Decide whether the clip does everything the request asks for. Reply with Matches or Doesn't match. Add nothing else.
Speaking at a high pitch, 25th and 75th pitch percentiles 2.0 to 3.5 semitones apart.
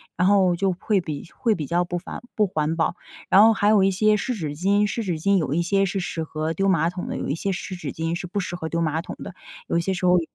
Doesn't match